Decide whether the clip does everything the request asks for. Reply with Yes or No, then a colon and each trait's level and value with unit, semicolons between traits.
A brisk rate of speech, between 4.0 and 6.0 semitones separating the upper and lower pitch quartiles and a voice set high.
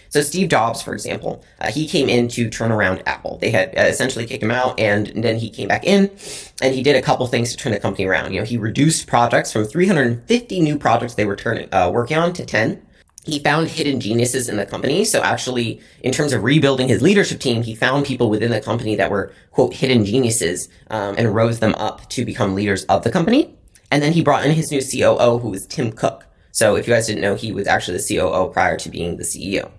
No: fast, 245 wpm; average, 4.5 semitones; low, 120 Hz